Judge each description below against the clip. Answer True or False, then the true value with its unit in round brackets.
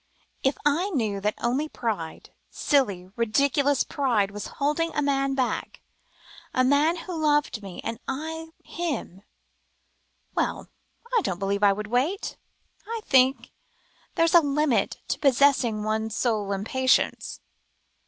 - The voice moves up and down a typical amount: False (5.7 semitones)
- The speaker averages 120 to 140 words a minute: True (135 wpm)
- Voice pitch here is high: True (260 Hz)